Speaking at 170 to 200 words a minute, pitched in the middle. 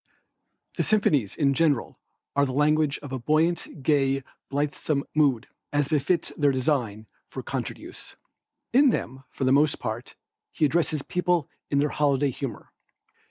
No: average, 150 wpm; medium, 145 Hz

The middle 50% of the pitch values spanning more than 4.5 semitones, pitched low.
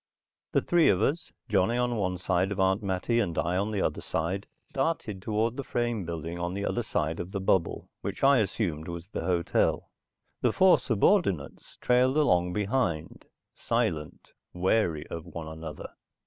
Yes: average, 5.3 semitones; very low, 95 Hz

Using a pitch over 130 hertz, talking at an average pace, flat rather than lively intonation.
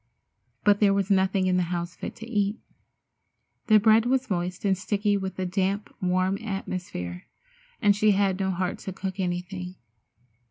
Yes: high, 190 Hz; average, 165 wpm; narrow, 2.0 semitones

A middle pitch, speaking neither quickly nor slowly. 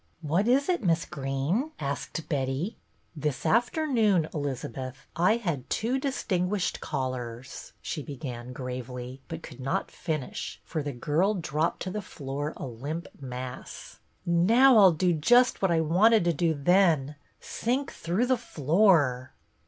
Yes: medium, 160 Hz; average, 160 wpm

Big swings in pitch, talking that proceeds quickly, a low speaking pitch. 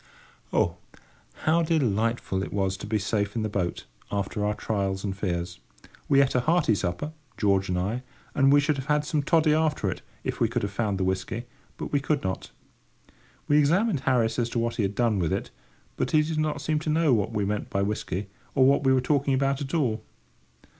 Yes: wide, 6.6 semitones; fast, 215 wpm; low, 120 Hz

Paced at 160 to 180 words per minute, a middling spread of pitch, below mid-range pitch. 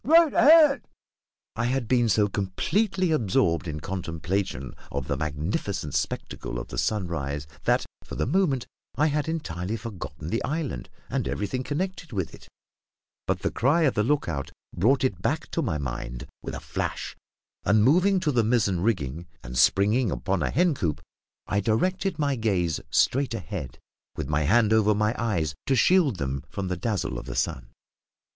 No: average, 170 wpm; wide, 8.9 semitones; low, 105 Hz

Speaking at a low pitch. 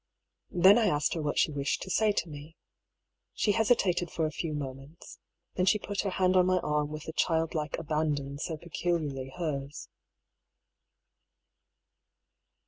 No: medium, 160 Hz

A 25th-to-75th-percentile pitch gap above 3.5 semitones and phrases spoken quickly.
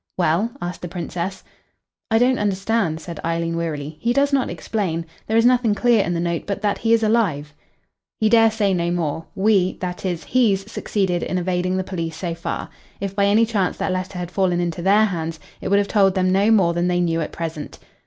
Yes: average, 3.9 semitones; fast, 215 wpm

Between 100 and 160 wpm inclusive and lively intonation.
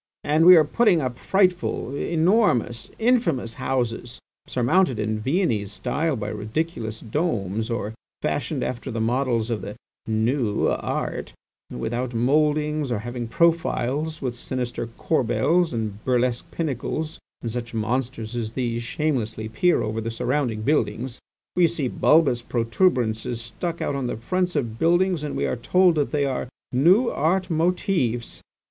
Yes: average, 140 wpm; wide, 5.8 semitones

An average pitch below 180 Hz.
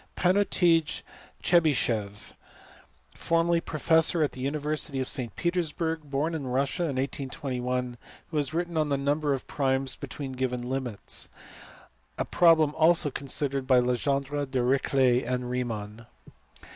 Yes: medium, 140 Hz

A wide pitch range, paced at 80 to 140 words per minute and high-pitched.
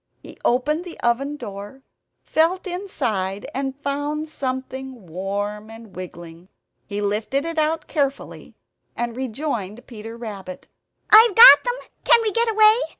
Yes: wide, 7.1 semitones; slow, 135 wpm; very high, 260 Hz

